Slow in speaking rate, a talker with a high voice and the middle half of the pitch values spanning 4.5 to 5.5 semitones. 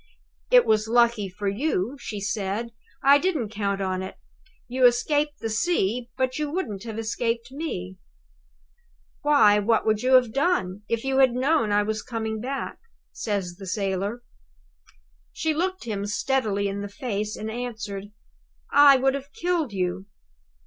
No: average, 155 wpm; high, 225 Hz; average, 4.8 semitones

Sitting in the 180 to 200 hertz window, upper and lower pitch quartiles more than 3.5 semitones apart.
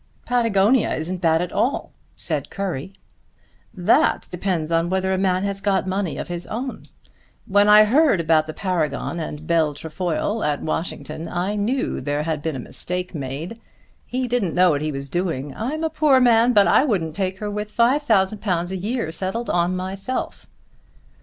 Yes: medium, 185 Hz; average, 4.4 semitones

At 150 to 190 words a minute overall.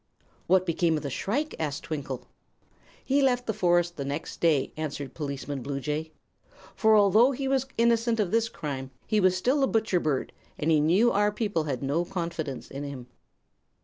Yes: average, 180 wpm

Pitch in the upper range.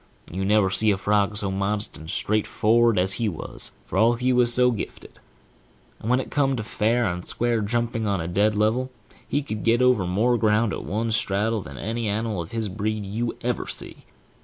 No: low, 110 Hz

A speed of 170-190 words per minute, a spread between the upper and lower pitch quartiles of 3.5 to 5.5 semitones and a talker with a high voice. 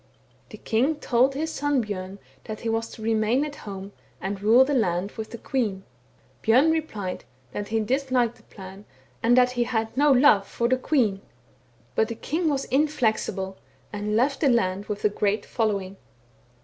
Yes: average, 175 wpm; average, 4.4 semitones; high, 225 Hz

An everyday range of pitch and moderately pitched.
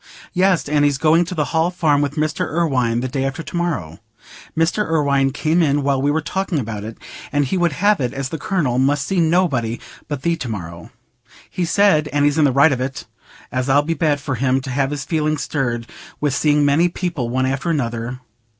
Yes: average, 3.8 semitones; medium, 145 Hz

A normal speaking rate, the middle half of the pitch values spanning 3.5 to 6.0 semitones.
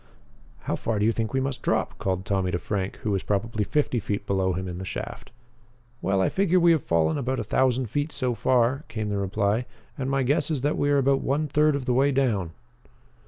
No: fast, 230 wpm; wide, 5.6 semitones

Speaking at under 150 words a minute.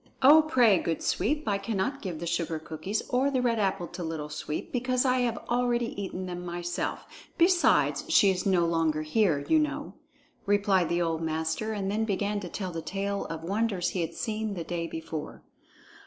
No: average, 190 wpm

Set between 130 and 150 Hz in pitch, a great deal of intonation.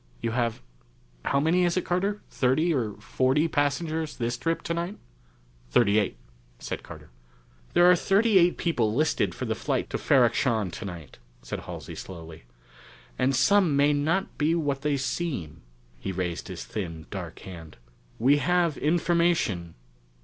Yes: medium, 140 Hz; wide, 7.8 semitones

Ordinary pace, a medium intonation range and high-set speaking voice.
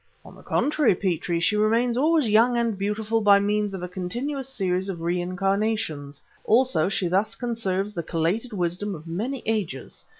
Yes: average, 165 wpm; average, 4.2 semitones; high, 205 Hz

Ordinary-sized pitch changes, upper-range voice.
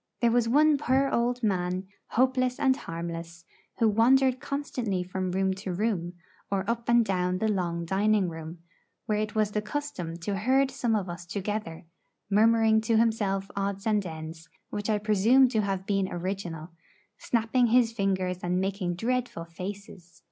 Yes: average, 4.2 semitones; high, 205 Hz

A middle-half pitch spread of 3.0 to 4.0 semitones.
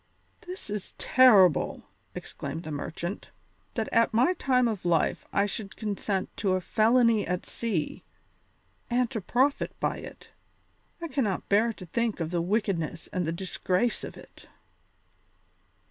No: average, 4.5 semitones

